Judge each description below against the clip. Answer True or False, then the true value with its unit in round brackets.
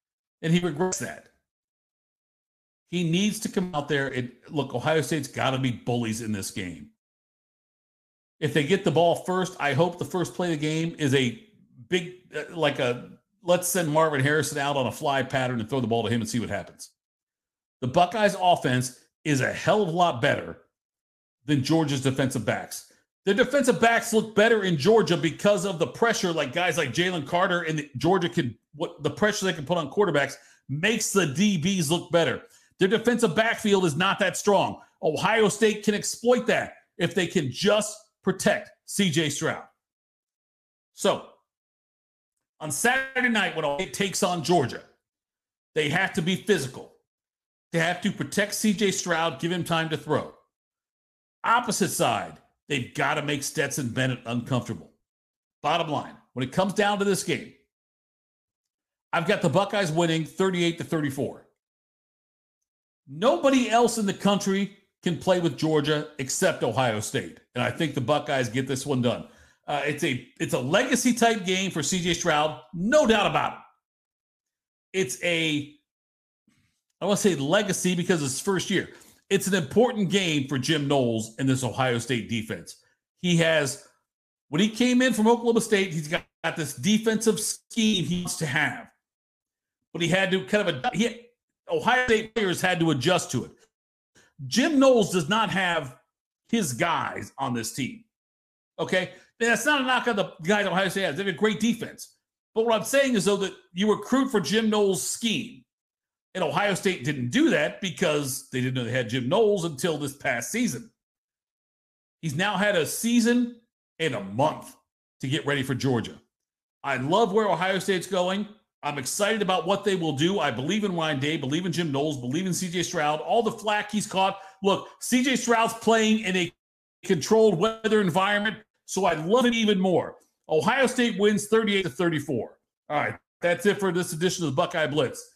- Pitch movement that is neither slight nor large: False (5.9 semitones)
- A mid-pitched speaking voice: True (175 Hz)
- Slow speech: False (180 wpm)